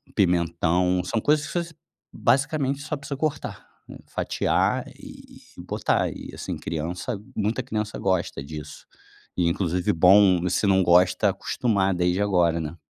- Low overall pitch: Yes, very low, 95 Hz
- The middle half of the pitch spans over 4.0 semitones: Yes, average, 4.6 semitones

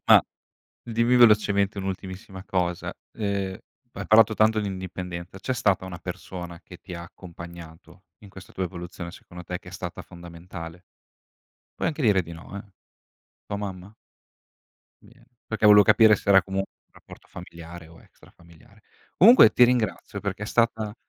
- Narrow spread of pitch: No, average, 3.3 semitones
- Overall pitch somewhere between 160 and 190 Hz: No, very low, 95 Hz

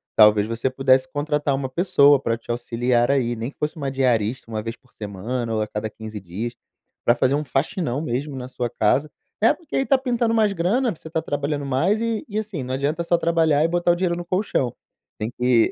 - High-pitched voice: No, low, 135 Hz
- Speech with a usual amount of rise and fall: No, wide, 6.1 semitones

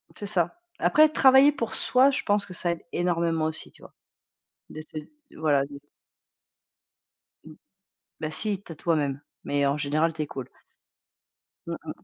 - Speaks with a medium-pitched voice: Yes, medium, 165 Hz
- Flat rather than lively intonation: No, wide, 5.4 semitones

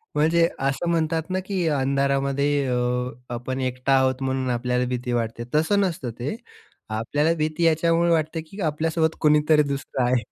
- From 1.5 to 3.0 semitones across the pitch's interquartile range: No, average, 3.9 semitones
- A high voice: No, medium, 145 Hz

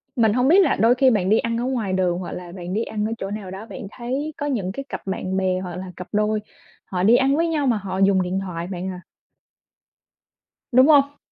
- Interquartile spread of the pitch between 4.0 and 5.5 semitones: Yes, average, 5.2 semitones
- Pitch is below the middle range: No, high, 210 Hz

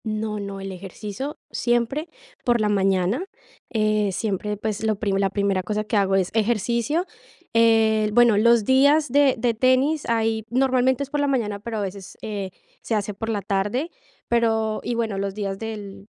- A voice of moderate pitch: No, high, 220 Hz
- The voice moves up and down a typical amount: Yes, average, 3.0 semitones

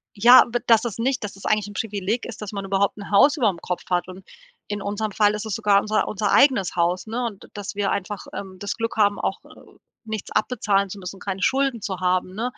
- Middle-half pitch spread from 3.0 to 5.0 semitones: No, narrow, 2.4 semitones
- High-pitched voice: Yes, high, 205 Hz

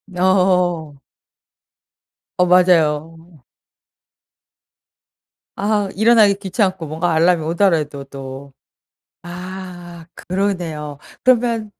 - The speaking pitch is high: No, medium, 175 Hz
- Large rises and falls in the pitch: No, average, 3.2 semitones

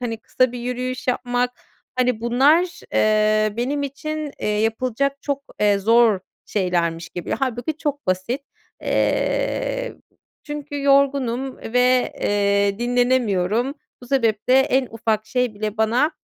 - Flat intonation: No, average, 4.2 semitones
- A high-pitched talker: Yes, high, 245 Hz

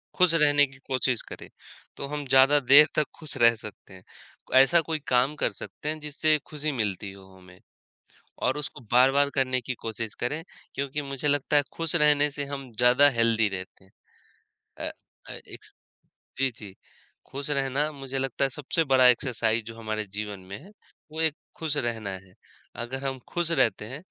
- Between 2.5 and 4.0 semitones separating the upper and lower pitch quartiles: No, average, 4.4 semitones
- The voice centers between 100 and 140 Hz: Yes, low, 135 Hz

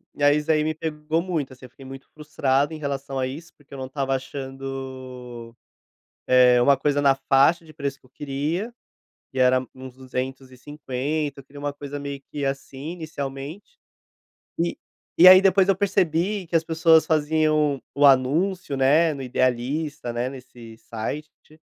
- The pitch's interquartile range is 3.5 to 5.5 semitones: No, average, 2.9 semitones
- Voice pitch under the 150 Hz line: Yes, medium, 140 Hz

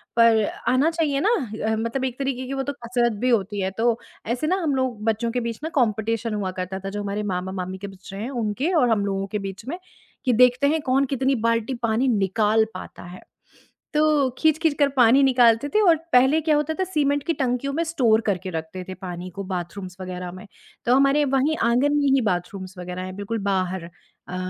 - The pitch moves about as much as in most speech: No, wide, 5.8 semitones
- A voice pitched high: Yes, high, 230 Hz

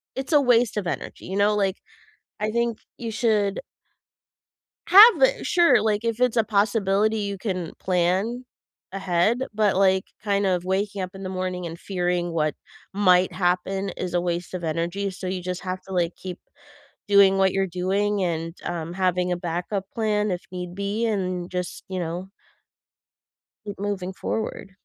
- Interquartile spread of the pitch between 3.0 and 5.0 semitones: No, narrow, 2.6 semitones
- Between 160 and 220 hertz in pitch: Yes, high, 190 Hz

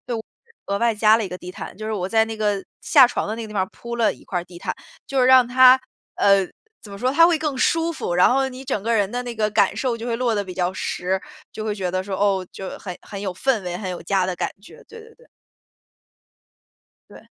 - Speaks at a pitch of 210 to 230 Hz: Yes, high, 215 Hz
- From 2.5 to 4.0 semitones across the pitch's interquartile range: No, average, 4.7 semitones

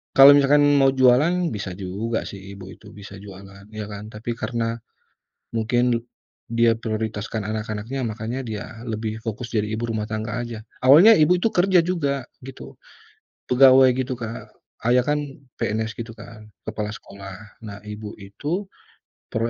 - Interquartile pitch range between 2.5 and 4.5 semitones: Yes, average, 3.5 semitones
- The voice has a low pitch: Yes, low, 115 Hz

